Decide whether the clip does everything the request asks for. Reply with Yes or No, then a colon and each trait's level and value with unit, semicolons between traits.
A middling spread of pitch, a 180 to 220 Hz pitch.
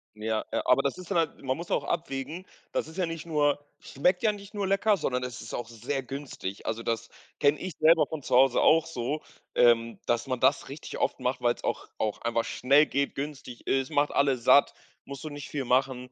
No: average, 4.2 semitones; medium, 140 Hz